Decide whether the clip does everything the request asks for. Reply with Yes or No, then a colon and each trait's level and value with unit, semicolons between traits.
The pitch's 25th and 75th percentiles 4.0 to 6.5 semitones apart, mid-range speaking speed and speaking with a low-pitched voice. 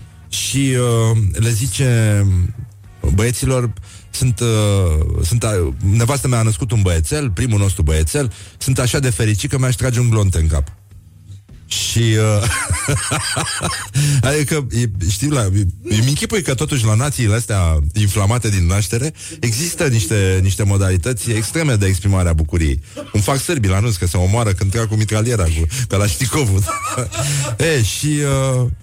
Yes: average, 4.5 semitones; average, 145 wpm; low, 110 Hz